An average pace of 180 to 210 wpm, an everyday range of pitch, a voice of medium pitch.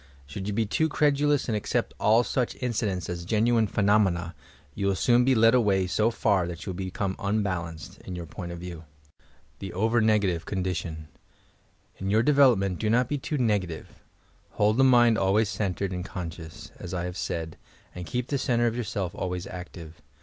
No: average, 185 wpm; average, 4.4 semitones; low, 100 Hz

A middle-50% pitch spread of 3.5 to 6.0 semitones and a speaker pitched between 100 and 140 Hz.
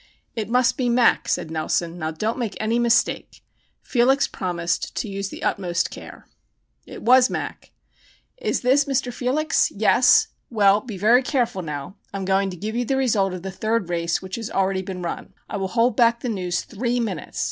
No: average, 4.6 semitones; high, 215 Hz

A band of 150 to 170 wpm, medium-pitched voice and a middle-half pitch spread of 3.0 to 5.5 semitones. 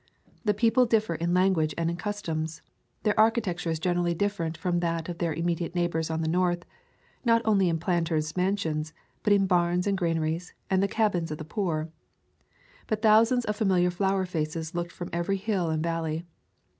No: average, 180 wpm; medium, 175 Hz; average, 3.4 semitones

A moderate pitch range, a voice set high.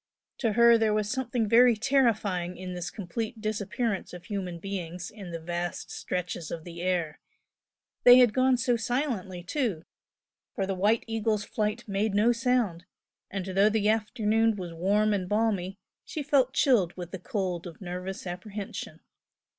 Yes: average, 4.0 semitones; high, 205 Hz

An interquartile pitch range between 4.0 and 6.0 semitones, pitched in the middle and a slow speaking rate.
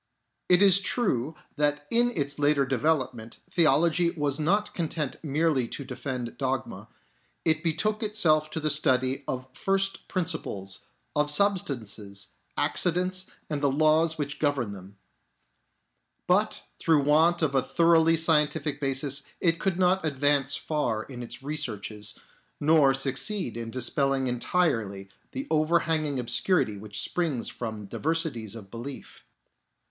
Yes: average, 4.4 semitones; medium, 150 Hz; slow, 130 wpm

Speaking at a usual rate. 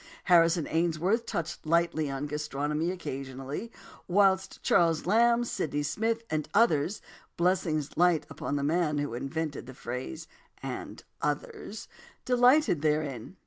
No: slow, 120 wpm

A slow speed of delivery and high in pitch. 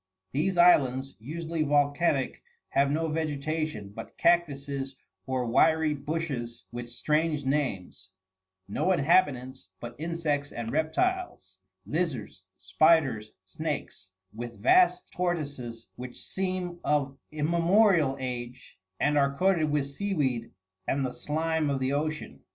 No: slow, 115 wpm; medium, 145 Hz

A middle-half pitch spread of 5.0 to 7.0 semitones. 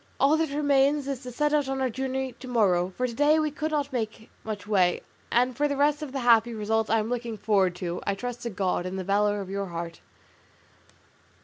Yes: wide, 5.5 semitones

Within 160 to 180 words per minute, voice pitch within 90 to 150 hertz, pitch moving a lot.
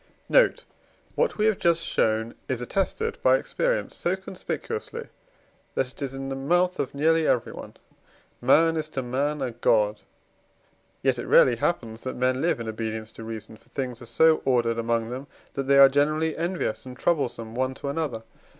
Yes: average, 175 wpm; low, 135 Hz; wide, 5.7 semitones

